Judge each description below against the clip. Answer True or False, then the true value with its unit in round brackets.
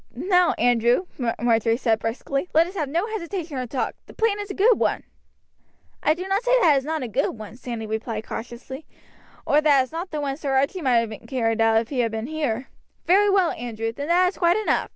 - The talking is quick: True (235 wpm)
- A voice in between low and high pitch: False (275 Hz)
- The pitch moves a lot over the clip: True (7.1 semitones)